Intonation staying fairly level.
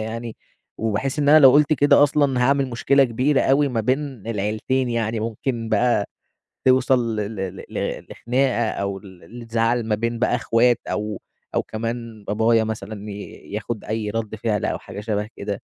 No: average, 3.0 semitones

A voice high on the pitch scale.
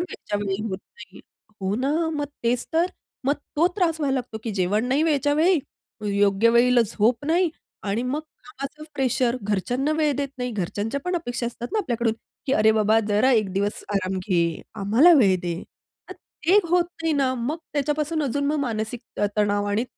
Yes: high, 245 Hz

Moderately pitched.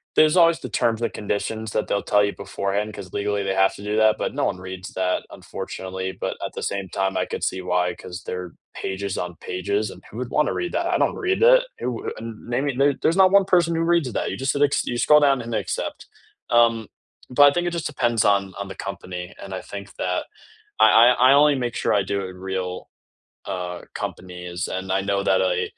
No: low, 100 Hz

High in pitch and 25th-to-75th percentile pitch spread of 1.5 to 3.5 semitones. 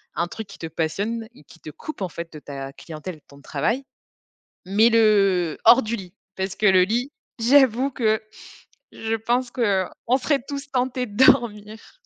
No: high, 215 Hz; average, 5.2 semitones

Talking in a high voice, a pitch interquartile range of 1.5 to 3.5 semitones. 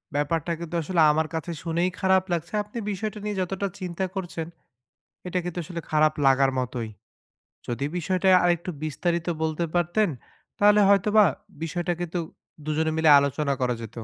No: medium, 170 Hz; average, 3.2 semitones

